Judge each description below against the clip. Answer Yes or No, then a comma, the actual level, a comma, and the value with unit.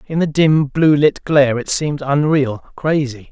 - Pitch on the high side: No, medium, 145 Hz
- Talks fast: No, average, 180 wpm